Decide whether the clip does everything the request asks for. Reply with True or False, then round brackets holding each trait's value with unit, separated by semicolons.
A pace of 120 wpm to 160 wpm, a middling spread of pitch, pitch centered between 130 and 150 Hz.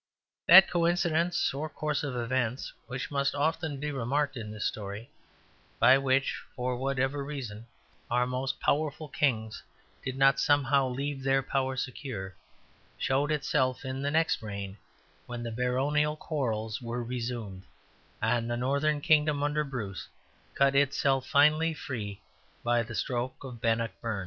True (140 wpm; 3.4 semitones; 135 Hz)